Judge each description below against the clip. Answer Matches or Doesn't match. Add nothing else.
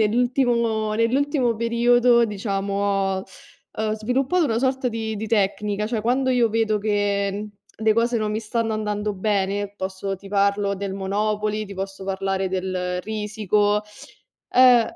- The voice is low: Doesn't match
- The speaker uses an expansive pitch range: Doesn't match